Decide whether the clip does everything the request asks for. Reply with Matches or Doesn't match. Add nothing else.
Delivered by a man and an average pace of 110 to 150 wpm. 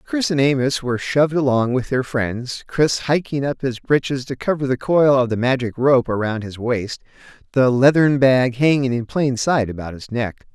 Doesn't match